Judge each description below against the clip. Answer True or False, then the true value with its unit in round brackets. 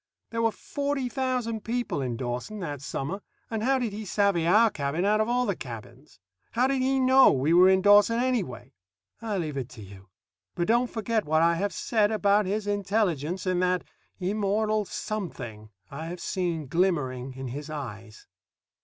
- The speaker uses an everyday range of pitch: False (7.2 semitones)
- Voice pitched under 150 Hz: False (190 Hz)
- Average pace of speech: True (180 wpm)